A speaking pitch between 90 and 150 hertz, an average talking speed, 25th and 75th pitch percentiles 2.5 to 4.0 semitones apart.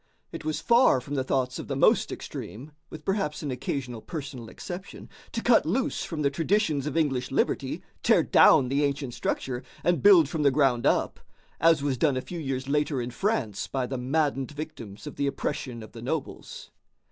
Yes: medium, 140 Hz; average, 195 wpm; average, 3.6 semitones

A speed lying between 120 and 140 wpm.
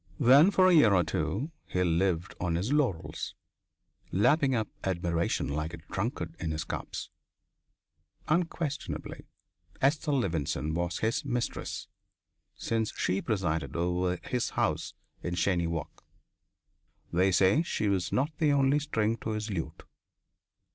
Yes: slow, 135 wpm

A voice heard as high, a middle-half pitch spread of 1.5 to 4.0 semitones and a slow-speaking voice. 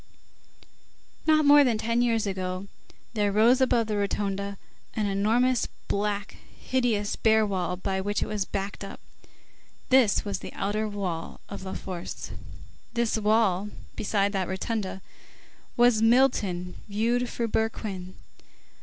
Yes: high, 210 Hz; average, 2.8 semitones; slow, 130 wpm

